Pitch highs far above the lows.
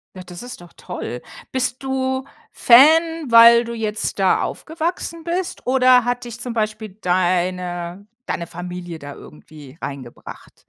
Yes: wide, 6.6 semitones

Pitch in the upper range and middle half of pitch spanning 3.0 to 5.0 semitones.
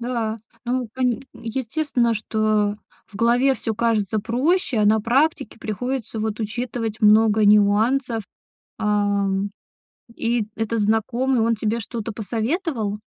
No: high, 225 Hz; narrow, 2.4 semitones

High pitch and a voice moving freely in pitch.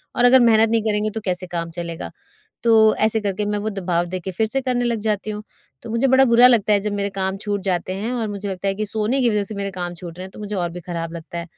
No: high, 205 Hz; average, 3.3 semitones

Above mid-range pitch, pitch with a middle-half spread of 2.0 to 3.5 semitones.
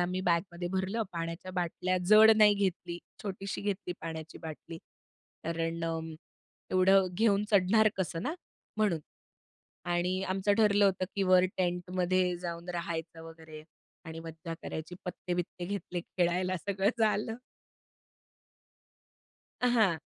No: medium, 180 Hz; average, 2.9 semitones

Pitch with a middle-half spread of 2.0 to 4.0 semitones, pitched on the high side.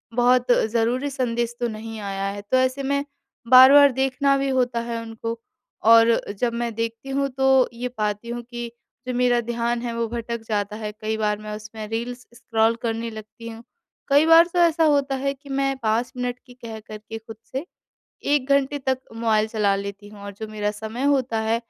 Yes: average, 2.9 semitones; high, 235 Hz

